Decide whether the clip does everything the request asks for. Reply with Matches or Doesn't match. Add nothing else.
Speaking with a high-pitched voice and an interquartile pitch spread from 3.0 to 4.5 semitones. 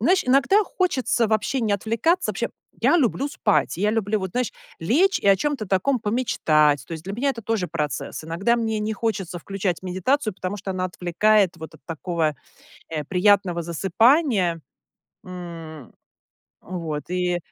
Doesn't match